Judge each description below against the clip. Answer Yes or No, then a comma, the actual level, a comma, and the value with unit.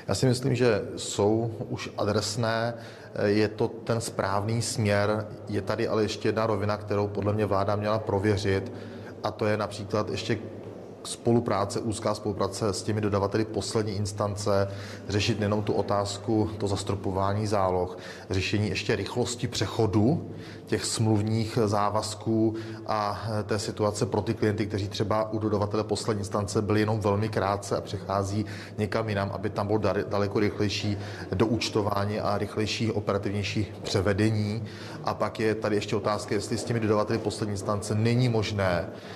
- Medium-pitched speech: No, low, 105 Hz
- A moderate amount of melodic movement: No, narrow, 1.4 semitones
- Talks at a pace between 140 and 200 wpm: Yes, average, 145 wpm